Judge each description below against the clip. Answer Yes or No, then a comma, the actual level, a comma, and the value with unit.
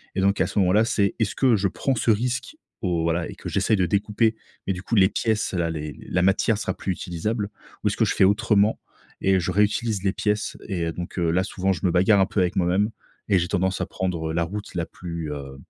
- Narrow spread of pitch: No, average, 3.2 semitones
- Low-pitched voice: Yes, very low, 95 Hz